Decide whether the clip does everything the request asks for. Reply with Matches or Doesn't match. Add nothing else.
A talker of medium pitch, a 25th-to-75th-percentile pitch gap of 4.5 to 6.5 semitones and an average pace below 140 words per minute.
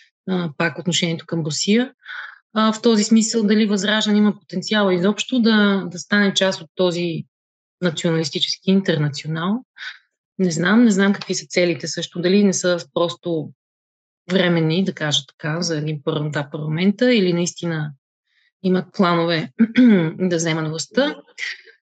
Doesn't match